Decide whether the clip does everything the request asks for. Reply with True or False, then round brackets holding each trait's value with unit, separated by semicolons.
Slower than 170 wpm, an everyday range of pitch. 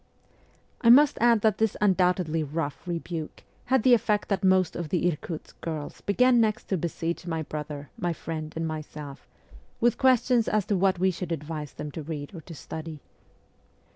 False (175 wpm; 5.0 semitones)